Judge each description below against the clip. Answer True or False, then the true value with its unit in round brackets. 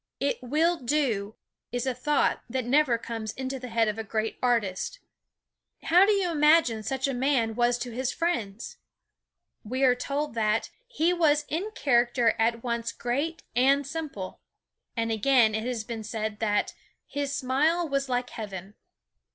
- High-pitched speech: True (250 Hz)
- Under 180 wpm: True (160 wpm)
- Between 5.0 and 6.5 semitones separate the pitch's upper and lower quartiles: False (4.3 semitones)